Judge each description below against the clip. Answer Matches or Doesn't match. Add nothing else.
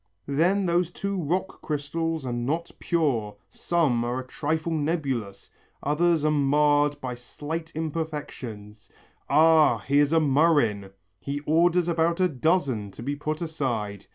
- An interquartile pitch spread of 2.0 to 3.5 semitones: Doesn't match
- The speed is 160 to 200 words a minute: Doesn't match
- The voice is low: Doesn't match